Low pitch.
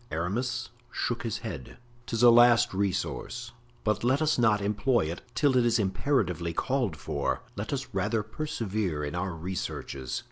Yes: low, 110 Hz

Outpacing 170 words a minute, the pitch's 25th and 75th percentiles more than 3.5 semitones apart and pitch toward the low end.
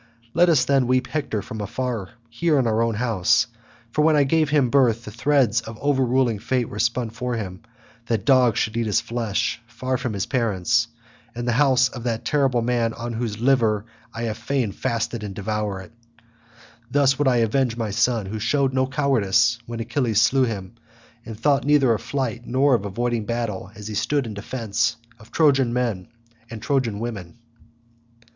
No: average, 185 wpm; average, 3.0 semitones; low, 120 Hz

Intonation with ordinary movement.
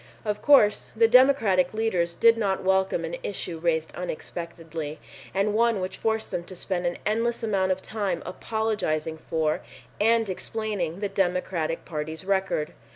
Yes: average, 4.3 semitones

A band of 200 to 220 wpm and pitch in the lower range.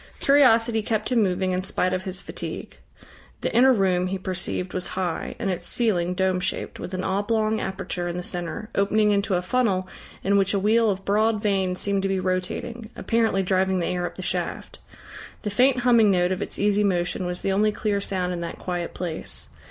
No: fast, 205 wpm; high, 195 Hz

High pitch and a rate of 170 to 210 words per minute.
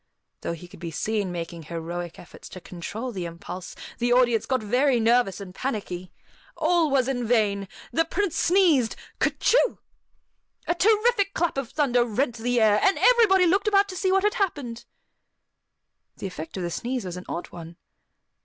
Yes: high, 240 Hz; average, 175 wpm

